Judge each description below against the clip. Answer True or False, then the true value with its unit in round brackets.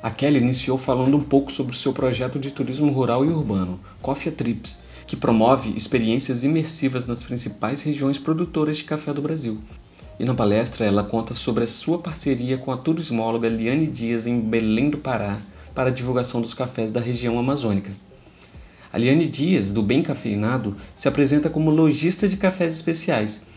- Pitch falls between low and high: False (125 Hz)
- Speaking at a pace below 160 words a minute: False (175 wpm)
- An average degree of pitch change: True (4.4 semitones)